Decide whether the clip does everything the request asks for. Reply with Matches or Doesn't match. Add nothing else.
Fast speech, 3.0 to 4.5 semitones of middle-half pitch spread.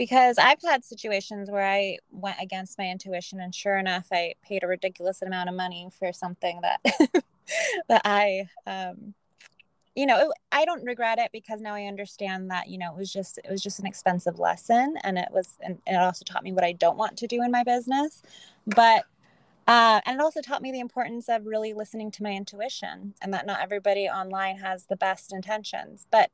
Matches